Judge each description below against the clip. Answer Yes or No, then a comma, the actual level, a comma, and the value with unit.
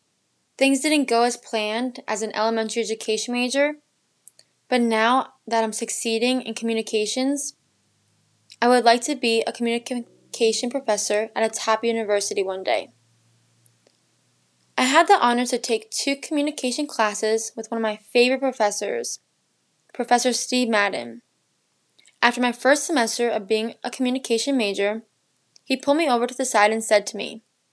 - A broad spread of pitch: No, average, 2.8 semitones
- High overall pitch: Yes, high, 230 Hz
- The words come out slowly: No, average, 150 wpm